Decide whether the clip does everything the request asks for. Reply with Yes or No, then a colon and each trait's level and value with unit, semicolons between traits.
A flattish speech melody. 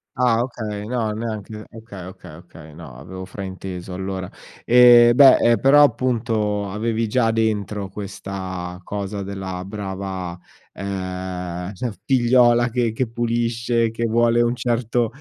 No: average, 3.9 semitones